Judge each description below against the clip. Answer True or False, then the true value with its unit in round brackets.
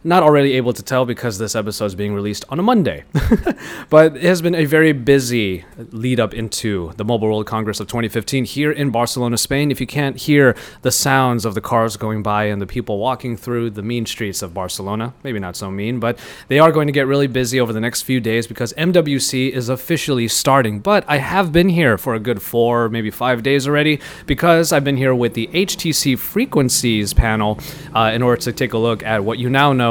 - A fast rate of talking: True (225 wpm)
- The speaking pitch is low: True (125 Hz)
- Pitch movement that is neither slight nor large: True (4.1 semitones)